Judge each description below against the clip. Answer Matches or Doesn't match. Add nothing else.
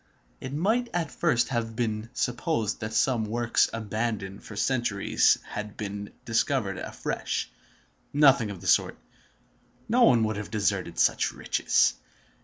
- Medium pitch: Doesn't match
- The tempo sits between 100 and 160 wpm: Matches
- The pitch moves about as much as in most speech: Matches